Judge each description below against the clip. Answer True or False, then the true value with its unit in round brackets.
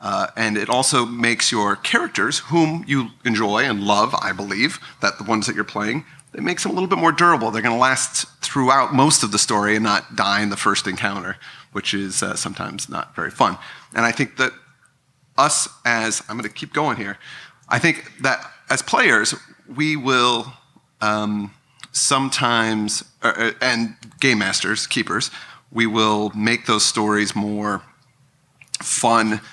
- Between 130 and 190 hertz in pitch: False (115 Hz)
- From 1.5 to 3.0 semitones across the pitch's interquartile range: False (4.2 semitones)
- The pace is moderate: True (170 wpm)